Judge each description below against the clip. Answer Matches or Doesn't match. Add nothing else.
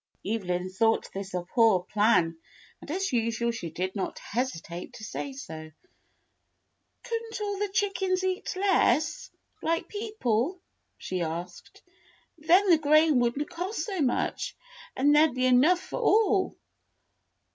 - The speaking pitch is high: Matches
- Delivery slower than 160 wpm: Matches